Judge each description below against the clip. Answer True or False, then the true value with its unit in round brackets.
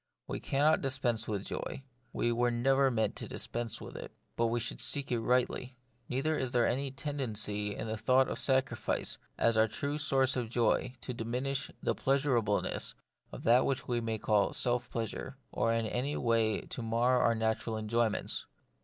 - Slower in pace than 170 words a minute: False (180 wpm)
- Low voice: True (120 Hz)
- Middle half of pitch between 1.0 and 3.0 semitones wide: True (2.7 semitones)